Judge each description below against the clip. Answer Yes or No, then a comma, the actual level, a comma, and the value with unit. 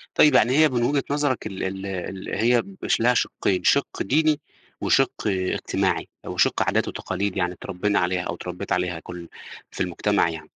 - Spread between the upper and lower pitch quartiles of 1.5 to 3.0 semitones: No, wide, 5.6 semitones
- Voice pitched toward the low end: Yes, very low, 95 Hz